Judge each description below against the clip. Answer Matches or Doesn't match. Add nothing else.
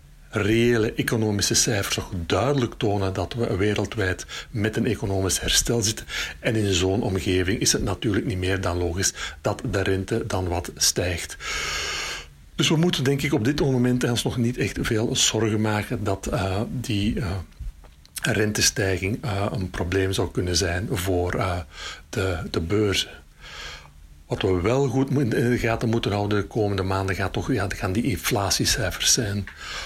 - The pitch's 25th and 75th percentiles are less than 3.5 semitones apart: Doesn't match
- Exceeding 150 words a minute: Matches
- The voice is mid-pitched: Doesn't match